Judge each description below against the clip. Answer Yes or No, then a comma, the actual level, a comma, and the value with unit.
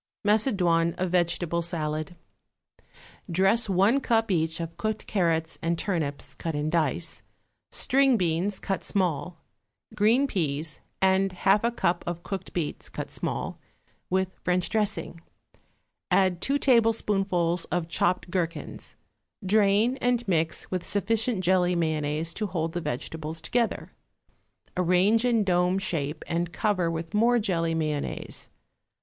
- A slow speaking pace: Yes, slow, 130 wpm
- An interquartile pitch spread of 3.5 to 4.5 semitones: Yes, average, 3.8 semitones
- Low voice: No, medium, 180 Hz